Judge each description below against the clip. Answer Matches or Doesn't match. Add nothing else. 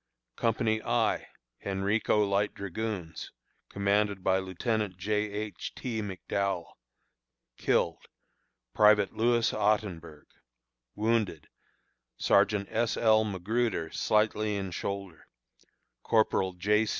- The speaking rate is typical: Doesn't match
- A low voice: Matches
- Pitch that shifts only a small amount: Matches